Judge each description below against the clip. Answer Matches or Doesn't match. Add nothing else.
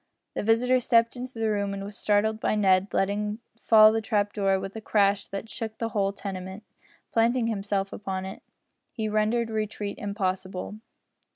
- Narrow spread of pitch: Matches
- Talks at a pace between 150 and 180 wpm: Matches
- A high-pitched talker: Matches